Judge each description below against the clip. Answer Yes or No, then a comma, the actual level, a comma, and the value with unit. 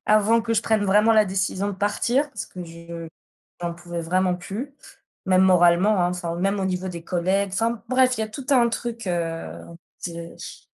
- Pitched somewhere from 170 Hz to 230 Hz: Yes, high, 190 Hz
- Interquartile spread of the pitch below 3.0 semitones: No, average, 3.9 semitones